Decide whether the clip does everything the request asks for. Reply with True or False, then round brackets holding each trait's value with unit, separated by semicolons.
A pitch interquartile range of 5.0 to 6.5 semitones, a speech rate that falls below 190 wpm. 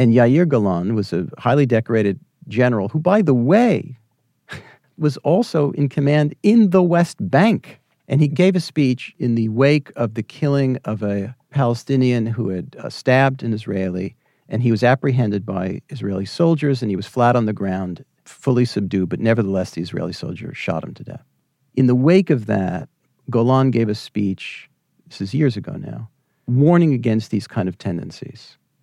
True (5.3 semitones; 175 wpm)